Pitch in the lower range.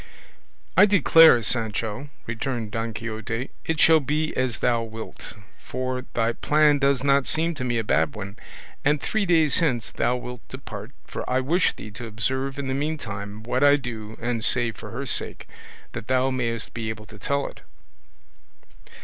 Yes: low, 125 Hz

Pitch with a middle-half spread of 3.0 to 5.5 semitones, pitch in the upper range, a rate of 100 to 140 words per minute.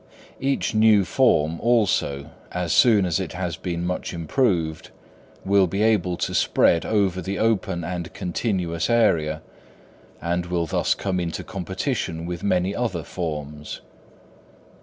No: average, 3.4 semitones; very low, 90 Hz; slow, 135 wpm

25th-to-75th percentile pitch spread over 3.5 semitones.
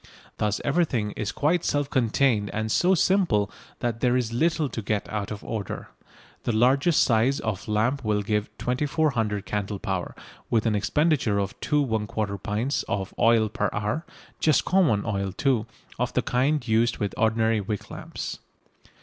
Yes: average, 4.7 semitones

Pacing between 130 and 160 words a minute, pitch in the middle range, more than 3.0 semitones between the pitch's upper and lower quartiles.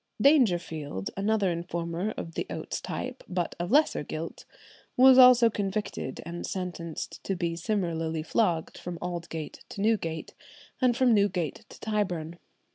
Yes: average, 140 wpm; medium, 180 Hz; average, 4.6 semitones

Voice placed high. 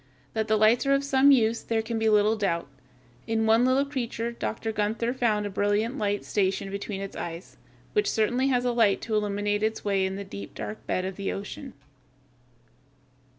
Yes: high, 220 Hz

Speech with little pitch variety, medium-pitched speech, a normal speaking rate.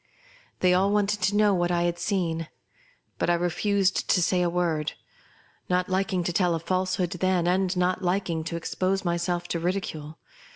Yes: narrow, 1.6 semitones; medium, 180 Hz; average, 180 wpm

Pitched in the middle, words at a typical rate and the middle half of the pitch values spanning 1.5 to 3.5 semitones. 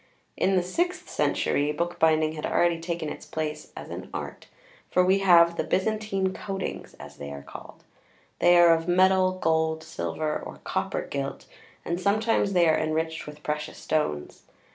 Yes: medium, 170 Hz; average, 165 wpm; average, 3.1 semitones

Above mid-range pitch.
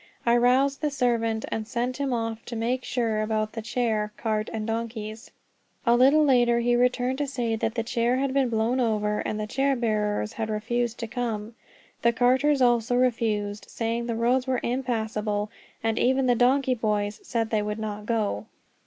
Yes: high, 235 Hz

